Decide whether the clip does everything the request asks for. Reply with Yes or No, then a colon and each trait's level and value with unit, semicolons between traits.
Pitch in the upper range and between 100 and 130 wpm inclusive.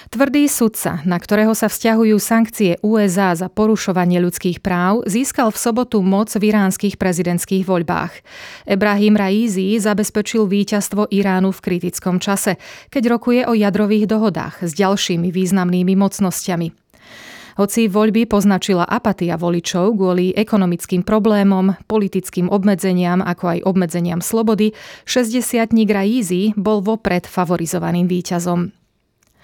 Yes: high, 200 Hz; average, 120 wpm